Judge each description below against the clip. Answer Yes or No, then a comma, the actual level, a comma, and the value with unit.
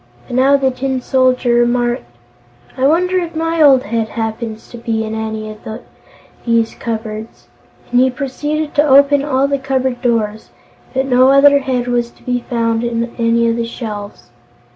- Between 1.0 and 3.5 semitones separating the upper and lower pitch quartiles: Yes, average, 2.9 semitones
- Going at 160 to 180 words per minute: Yes, average, 170 wpm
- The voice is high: Yes, high, 245 Hz